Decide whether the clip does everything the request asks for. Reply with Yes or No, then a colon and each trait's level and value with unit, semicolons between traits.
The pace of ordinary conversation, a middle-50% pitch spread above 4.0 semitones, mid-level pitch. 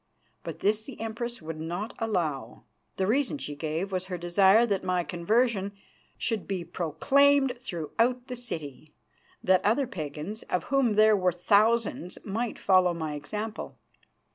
No: average, 145 wpm; average, 5.0 semitones; high, 200 Hz